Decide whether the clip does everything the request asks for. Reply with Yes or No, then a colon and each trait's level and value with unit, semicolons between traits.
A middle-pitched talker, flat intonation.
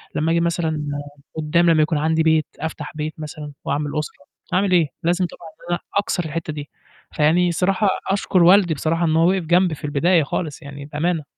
Yes: medium, 160 Hz; narrow, 2.3 semitones